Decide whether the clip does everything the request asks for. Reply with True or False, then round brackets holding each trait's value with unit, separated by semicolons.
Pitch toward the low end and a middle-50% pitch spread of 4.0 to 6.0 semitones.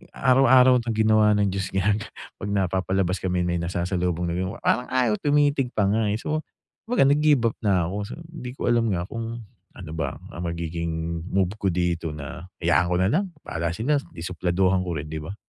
True (95 Hz; 5.2 semitones)